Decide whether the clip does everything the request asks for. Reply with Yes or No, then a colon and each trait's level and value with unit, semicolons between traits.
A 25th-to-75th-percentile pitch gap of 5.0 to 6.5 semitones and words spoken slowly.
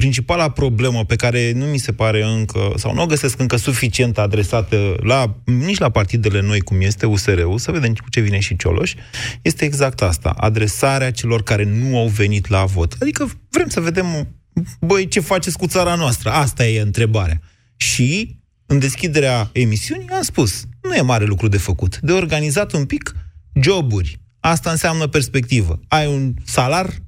No: wide, 5.6 semitones; fast, 175 wpm